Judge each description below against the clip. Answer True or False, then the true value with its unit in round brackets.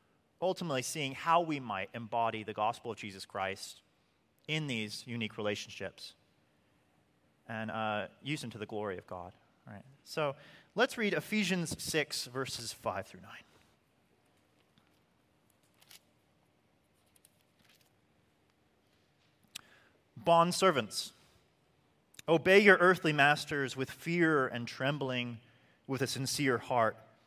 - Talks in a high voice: False (125 Hz)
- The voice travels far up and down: True (6.0 semitones)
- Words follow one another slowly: True (105 wpm)